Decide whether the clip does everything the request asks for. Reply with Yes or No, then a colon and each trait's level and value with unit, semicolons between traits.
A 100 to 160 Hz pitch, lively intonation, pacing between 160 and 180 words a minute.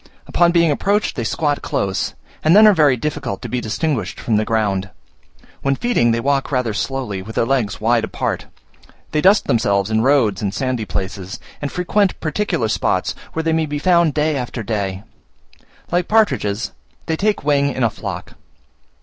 Yes: low, 135 Hz; wide, 6.5 semitones; average, 175 wpm